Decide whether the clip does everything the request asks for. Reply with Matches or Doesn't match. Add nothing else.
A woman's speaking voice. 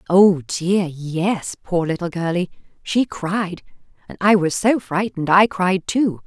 Matches